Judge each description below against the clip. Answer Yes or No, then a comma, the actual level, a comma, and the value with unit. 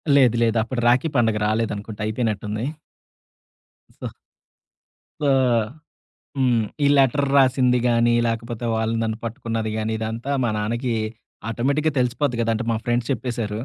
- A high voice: No, low, 115 Hz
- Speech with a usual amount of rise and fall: No, narrow, 2.1 semitones